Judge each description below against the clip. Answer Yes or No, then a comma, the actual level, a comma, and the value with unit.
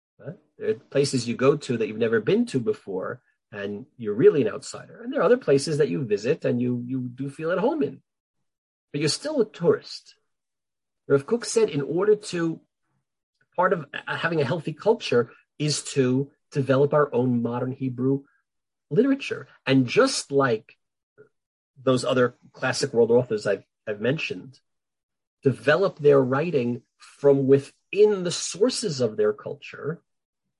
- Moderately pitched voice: Yes, medium, 145 Hz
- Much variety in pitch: Yes, wide, 8.5 semitones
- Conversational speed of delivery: Yes, average, 155 wpm